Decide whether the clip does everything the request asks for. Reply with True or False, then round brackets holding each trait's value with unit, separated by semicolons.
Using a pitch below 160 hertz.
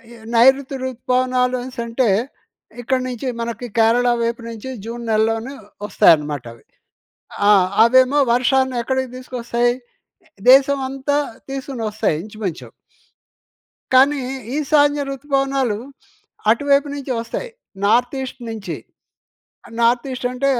False (250 Hz)